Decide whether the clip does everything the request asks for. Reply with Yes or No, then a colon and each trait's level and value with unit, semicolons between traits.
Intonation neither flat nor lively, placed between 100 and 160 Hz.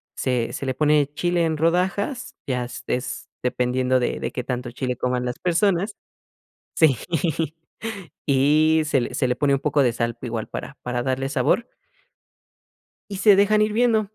No: wide, 5.8 semitones; medium, 140 Hz